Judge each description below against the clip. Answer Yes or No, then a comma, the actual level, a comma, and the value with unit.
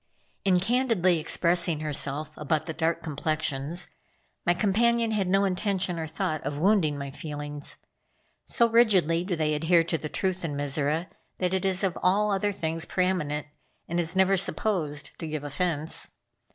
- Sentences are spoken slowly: No, average, 165 wpm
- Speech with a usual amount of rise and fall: Yes, average, 3.8 semitones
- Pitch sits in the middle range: Yes, medium, 170 Hz